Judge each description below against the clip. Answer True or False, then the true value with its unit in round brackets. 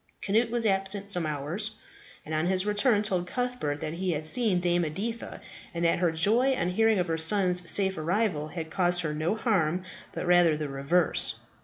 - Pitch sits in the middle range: True (180 Hz)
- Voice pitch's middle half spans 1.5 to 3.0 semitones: False (4.4 semitones)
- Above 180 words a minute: True (190 wpm)